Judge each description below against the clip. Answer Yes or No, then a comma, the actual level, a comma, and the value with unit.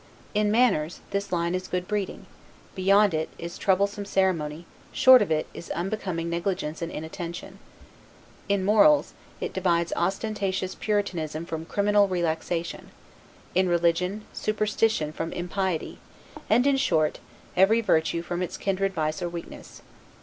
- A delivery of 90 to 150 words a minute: Yes, slow, 135 wpm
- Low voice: No, medium, 185 Hz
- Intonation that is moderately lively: Yes, average, 3.2 semitones